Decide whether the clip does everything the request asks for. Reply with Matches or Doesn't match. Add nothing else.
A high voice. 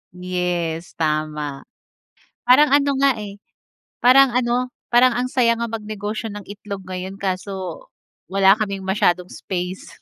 Matches